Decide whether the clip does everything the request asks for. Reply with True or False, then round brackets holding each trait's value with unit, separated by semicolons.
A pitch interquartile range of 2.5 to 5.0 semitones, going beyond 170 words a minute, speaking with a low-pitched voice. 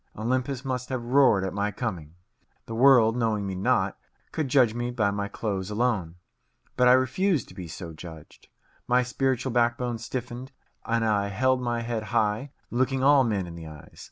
True (4.0 semitones; 180 wpm; 120 Hz)